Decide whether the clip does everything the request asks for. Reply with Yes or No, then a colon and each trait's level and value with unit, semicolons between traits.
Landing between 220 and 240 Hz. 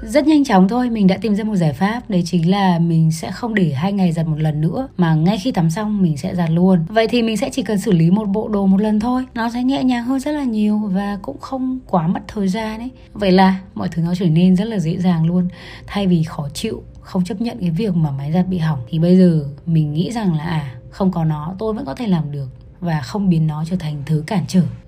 No: medium, 185 Hz